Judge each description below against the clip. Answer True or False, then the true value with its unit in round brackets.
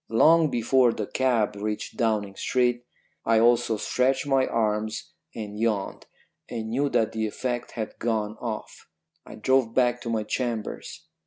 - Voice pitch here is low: True (115 Hz)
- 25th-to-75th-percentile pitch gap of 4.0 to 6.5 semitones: False (2.4 semitones)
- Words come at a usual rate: True (150 wpm)